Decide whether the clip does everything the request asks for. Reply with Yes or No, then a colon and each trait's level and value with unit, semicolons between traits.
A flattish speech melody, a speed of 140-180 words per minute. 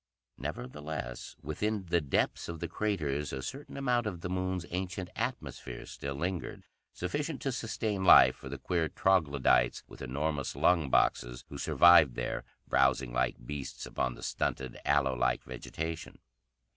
No: wide, 5.6 semitones; average, 145 wpm